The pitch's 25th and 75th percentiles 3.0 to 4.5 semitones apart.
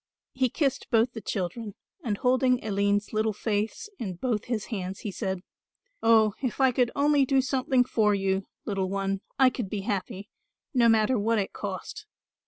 Yes: average, 4.1 semitones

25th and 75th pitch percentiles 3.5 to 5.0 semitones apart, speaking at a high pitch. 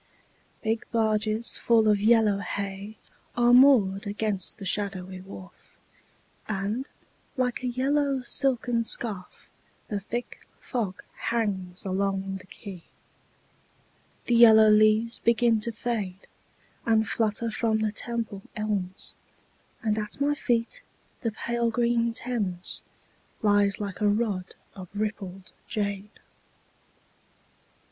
No: average, 2.9 semitones; high, 215 Hz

